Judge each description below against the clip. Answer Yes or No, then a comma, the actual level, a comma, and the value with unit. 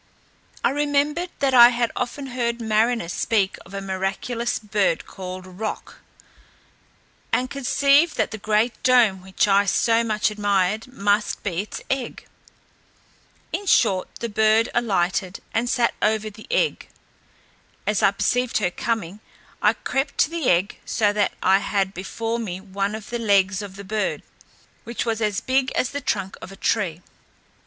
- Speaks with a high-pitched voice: Yes, high, 215 Hz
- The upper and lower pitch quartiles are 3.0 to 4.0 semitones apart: Yes, average, 3.6 semitones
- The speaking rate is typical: Yes, average, 160 wpm